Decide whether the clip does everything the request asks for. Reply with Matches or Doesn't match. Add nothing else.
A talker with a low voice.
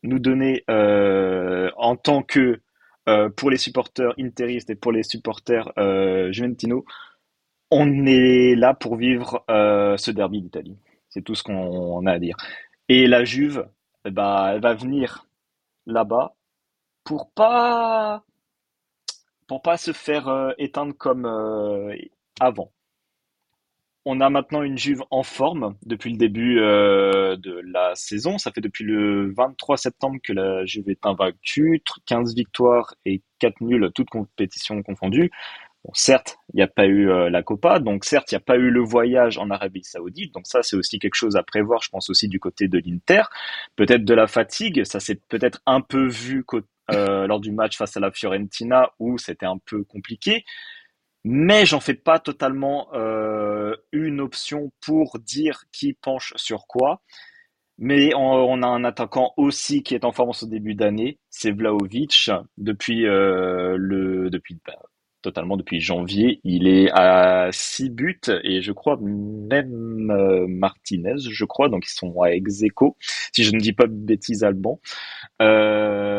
Matches